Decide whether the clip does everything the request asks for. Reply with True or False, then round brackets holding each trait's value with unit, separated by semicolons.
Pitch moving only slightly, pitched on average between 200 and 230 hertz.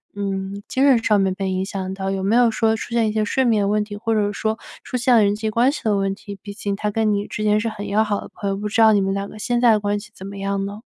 True (1.8 semitones; 210 Hz)